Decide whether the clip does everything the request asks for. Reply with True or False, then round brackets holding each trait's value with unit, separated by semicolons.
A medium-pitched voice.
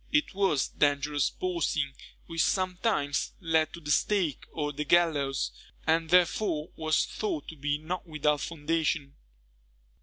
True (160 Hz)